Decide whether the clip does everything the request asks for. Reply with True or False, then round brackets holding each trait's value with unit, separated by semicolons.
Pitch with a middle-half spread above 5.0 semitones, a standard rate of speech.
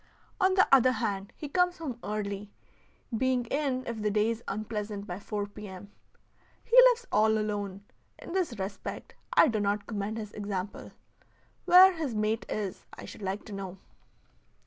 False (4.1 semitones; 170 wpm)